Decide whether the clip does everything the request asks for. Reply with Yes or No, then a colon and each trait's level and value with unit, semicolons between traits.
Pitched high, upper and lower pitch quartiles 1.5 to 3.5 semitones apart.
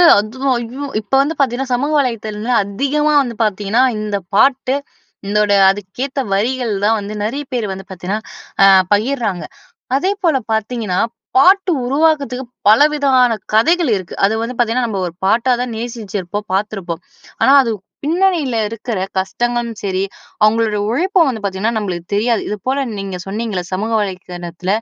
No: high, 230 Hz; average, 4.5 semitones